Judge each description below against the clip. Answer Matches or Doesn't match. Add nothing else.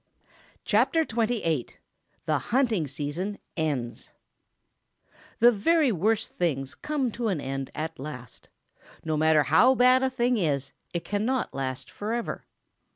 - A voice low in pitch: Doesn't match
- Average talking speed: Doesn't match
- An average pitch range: Doesn't match